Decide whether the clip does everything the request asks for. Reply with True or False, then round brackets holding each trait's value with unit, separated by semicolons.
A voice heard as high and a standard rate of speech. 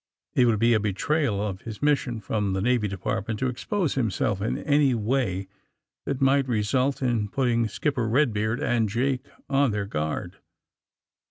False (115 Hz; 160 wpm)